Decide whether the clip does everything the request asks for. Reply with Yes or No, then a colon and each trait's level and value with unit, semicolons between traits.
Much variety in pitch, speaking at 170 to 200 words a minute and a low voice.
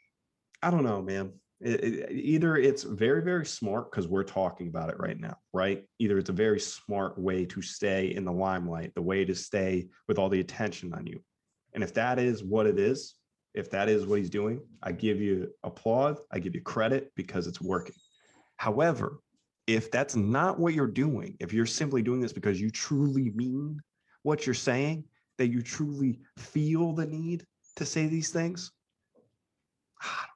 Yes: wide, 7.5 semitones; average, 190 wpm; low, 120 Hz